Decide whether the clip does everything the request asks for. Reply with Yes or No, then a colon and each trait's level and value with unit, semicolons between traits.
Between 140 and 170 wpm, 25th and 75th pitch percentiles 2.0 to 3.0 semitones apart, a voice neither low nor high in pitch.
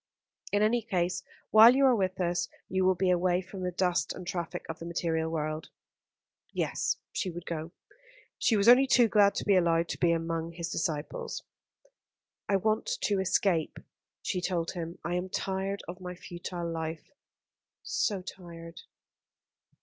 Yes: average, 165 wpm; narrow, 2.6 semitones; medium, 180 Hz